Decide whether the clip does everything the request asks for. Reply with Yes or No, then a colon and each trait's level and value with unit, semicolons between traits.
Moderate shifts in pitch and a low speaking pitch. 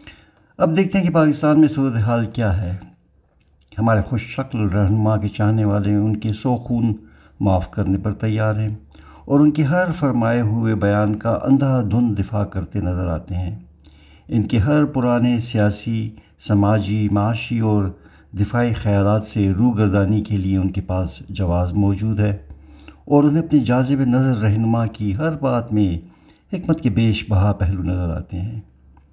Yes: average, 3.6 semitones; low, 105 Hz